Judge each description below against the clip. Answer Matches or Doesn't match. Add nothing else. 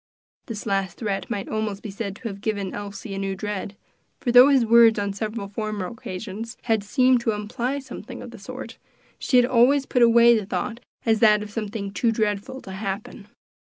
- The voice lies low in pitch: Doesn't match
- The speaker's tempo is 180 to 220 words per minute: Matches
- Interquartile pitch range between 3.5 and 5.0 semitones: Doesn't match